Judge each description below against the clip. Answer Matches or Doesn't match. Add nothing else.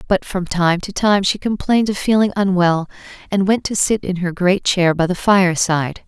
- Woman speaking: Matches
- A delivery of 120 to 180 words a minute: Doesn't match